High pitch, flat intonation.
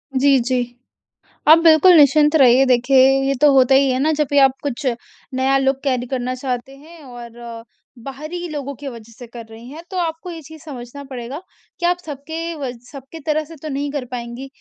No: very high, 270 Hz; average, 3.4 semitones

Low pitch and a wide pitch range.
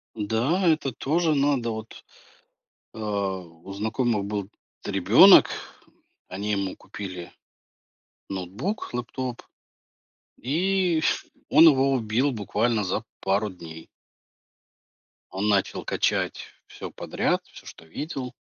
Yes: low, 110 Hz; wide, 5.7 semitones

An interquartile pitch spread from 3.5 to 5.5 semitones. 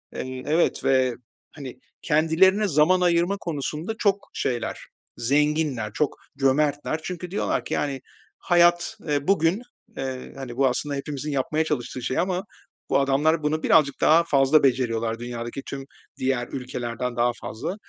Yes: average, 4.0 semitones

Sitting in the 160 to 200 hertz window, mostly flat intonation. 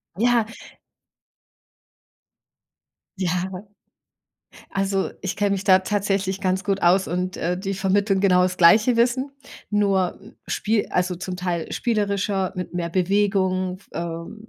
Yes: high, 190 Hz; narrow, 1.9 semitones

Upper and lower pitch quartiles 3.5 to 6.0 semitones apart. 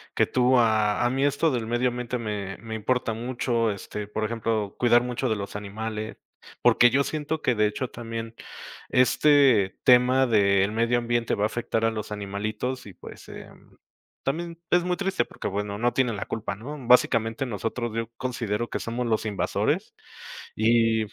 No: average, 2.8 semitones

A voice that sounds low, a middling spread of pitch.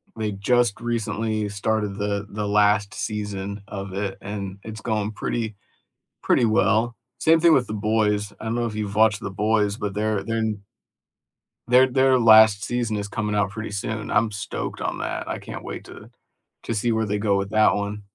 No: low, 105 Hz; narrow, 1.5 semitones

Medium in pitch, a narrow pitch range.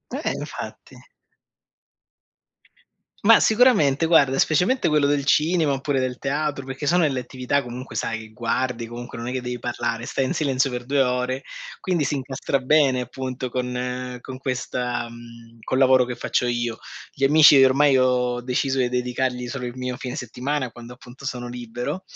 No: low, 130 Hz; narrow, 2.1 semitones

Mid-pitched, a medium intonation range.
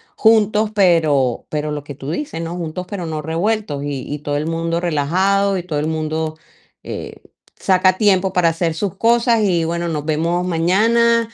Yes: medium, 170 Hz; average, 4.1 semitones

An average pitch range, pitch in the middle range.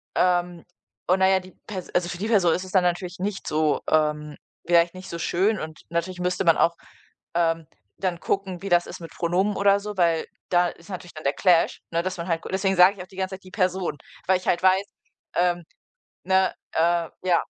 No: narrow, 1.9 semitones; medium, 180 Hz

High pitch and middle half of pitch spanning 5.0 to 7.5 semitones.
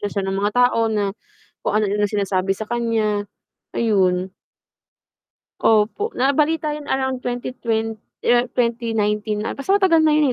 No: high, 225 Hz; average, 3.8 semitones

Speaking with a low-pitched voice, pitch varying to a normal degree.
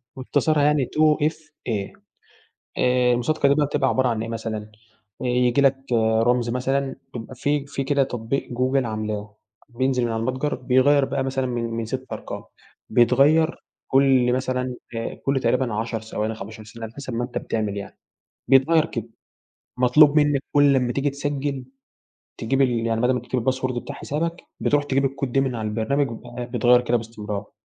Yes: low, 125 Hz; average, 3.1 semitones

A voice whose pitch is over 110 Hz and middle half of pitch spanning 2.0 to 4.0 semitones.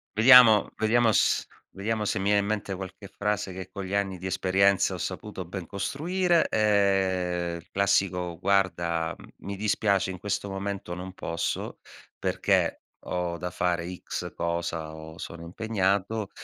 No: very low, 95 Hz; narrow, 2.5 semitones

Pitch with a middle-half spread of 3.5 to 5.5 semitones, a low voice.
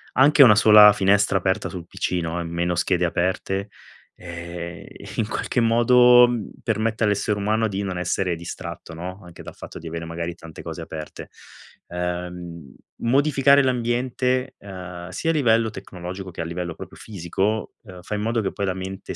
Yes: average, 4.4 semitones; very low, 95 Hz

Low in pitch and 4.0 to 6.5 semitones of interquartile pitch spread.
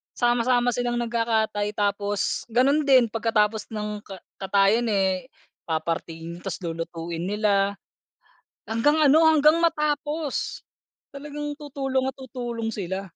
No: high, 230 Hz; average, 5.0 semitones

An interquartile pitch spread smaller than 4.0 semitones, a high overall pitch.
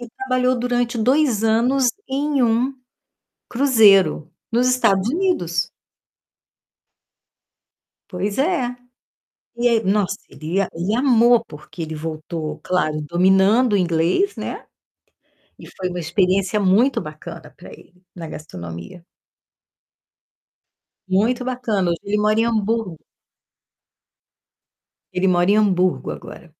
No: wide, 5.6 semitones; high, 210 Hz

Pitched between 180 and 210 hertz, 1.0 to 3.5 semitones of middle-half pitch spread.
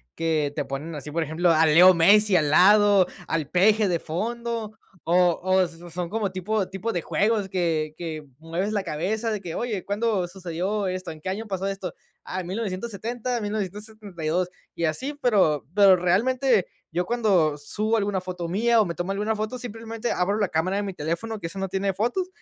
No: high, 190 Hz; average, 4.1 semitones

